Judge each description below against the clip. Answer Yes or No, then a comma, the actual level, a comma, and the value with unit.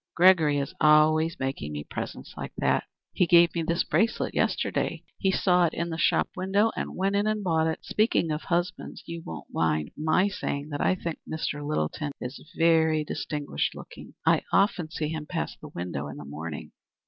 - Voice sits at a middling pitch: Yes, medium, 160 Hz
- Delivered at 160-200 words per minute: Yes, average, 190 wpm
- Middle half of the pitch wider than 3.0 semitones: Yes, average, 3.4 semitones